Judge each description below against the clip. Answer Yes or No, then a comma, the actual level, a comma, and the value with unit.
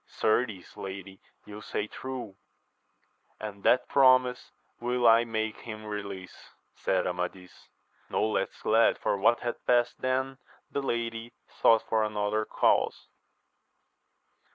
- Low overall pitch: Yes, low, 110 Hz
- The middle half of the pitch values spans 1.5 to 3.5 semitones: Yes, average, 2.9 semitones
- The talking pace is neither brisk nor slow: No, slow, 120 wpm